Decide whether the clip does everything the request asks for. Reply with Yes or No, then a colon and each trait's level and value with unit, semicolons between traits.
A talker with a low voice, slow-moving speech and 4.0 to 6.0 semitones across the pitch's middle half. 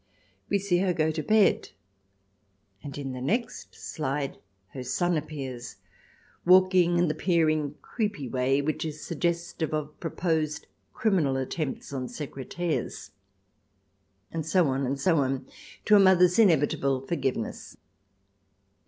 No: medium, 155 Hz; slow, 130 wpm; average, 4.4 semitones